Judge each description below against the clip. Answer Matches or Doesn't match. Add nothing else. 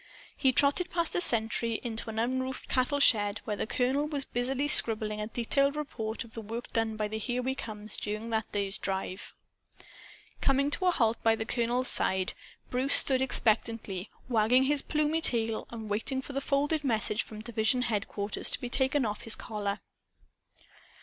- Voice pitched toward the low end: Doesn't match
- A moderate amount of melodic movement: Matches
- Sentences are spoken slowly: Doesn't match